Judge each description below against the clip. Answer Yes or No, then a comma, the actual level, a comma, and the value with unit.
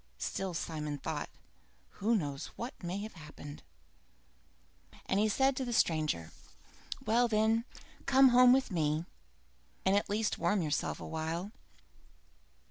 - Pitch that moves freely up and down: Yes, wide, 6.6 semitones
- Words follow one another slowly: Yes, slow, 125 wpm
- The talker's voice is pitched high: Yes, high, 195 Hz